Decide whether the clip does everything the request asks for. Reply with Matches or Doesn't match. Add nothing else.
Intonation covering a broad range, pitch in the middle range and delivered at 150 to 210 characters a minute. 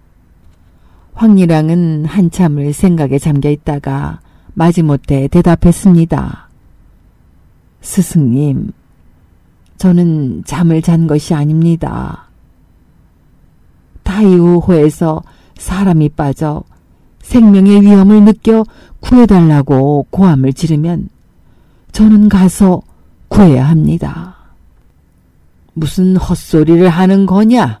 Matches